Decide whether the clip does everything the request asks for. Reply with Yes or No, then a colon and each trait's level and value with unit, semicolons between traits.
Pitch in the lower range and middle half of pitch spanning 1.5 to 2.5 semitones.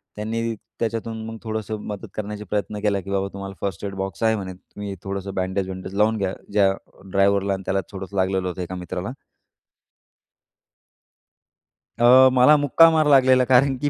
No: low, 100 Hz; average, 2.9 semitones